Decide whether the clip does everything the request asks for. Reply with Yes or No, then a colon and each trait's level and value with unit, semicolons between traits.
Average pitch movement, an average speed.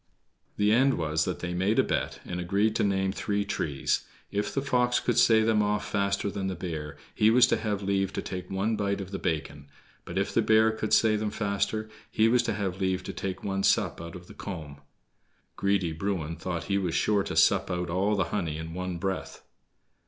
No: average, 3.1 semitones; fast, 220 wpm